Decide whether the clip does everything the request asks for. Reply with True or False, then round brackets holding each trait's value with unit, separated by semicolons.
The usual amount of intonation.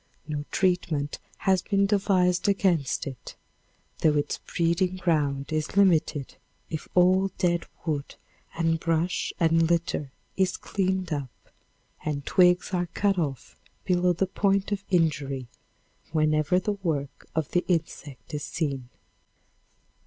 True (3.6 semitones)